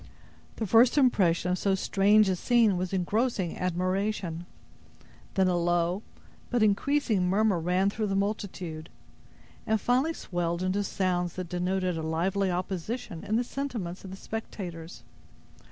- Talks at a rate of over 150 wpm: No, average, 140 wpm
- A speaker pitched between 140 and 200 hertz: Yes, high, 190 Hz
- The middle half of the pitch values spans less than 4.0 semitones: Yes, average, 3.4 semitones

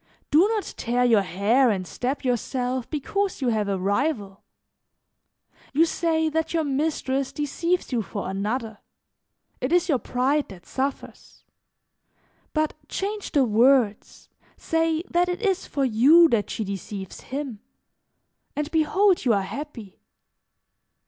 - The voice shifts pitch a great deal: Yes, wide, 6.5 semitones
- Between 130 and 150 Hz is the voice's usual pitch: No, very high, 270 Hz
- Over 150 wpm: No, slow, 135 wpm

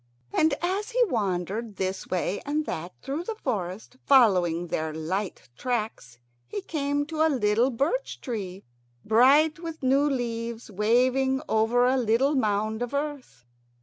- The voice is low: No, high, 245 Hz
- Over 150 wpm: No, average, 145 wpm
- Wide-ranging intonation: Yes, wide, 5.8 semitones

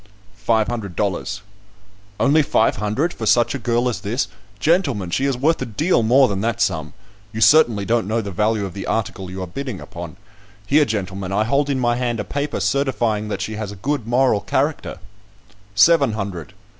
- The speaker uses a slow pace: No, average, 195 wpm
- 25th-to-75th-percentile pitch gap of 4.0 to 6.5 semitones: Yes, average, 4.6 semitones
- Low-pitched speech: Yes, low, 110 Hz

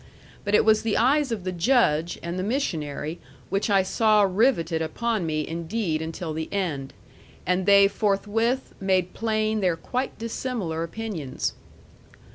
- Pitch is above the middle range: Yes, high, 195 Hz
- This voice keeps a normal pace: Yes, average, 145 wpm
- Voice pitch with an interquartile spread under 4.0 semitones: No, average, 5.2 semitones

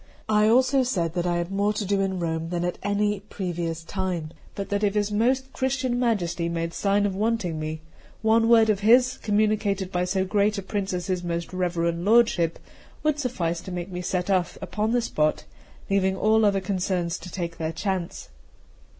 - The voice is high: Yes, high, 195 Hz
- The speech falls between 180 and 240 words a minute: Yes, average, 195 wpm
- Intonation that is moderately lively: Yes, average, 3.6 semitones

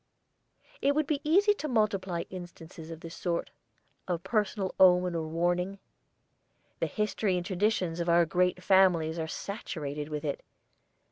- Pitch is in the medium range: Yes, medium, 180 Hz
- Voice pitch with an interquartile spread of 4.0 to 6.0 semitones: No, average, 3.6 semitones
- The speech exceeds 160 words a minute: No, average, 145 wpm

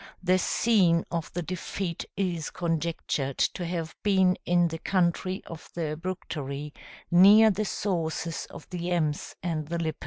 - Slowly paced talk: No, average, 150 wpm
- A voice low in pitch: No, medium, 170 Hz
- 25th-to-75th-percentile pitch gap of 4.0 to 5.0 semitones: No, narrow, 2.4 semitones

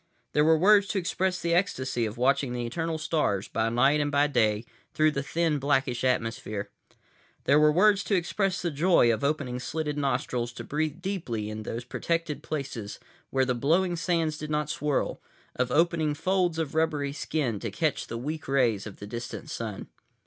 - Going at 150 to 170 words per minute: No, average, 185 wpm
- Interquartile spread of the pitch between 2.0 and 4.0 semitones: No, average, 5.0 semitones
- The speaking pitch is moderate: Yes, medium, 145 Hz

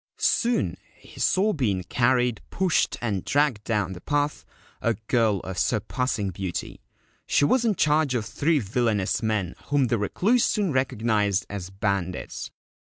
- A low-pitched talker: Yes, low, 115 Hz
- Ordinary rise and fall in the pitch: No, wide, 6.4 semitones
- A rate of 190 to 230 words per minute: No, average, 145 wpm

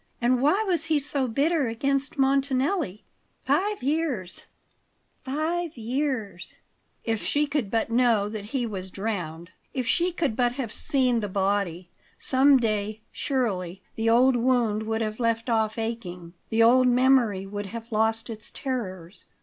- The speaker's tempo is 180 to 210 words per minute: No, average, 150 wpm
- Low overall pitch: No, high, 235 Hz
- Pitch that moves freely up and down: No, average, 4.4 semitones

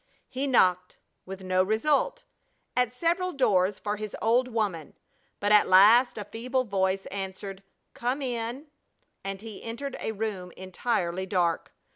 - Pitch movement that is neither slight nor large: Yes, average, 4.8 semitones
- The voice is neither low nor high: No, high, 210 Hz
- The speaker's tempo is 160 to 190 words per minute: No, average, 140 wpm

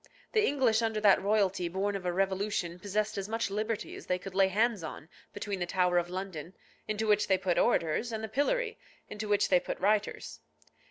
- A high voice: Yes, high, 200 Hz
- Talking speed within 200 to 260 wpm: Yes, fast, 205 wpm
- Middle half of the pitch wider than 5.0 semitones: No, average, 2.8 semitones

